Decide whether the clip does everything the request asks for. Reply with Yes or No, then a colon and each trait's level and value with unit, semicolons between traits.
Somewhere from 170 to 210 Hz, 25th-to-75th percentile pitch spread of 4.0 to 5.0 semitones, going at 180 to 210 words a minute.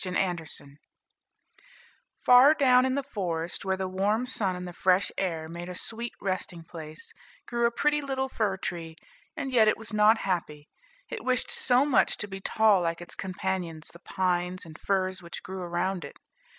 Yes: high, 190 Hz; average, 4.5 semitones; average, 185 wpm